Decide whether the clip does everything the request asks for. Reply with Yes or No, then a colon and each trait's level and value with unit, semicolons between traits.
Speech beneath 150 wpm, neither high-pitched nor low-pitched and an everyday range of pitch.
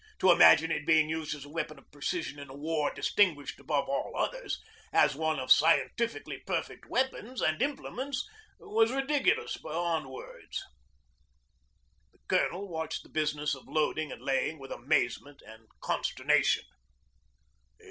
Yes: average, 140 wpm; medium, 155 Hz; average, 4.4 semitones